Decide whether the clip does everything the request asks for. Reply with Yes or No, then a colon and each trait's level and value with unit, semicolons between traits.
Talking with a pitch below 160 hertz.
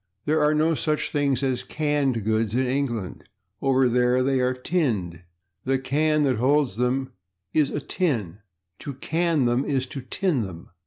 Yes: low, 135 Hz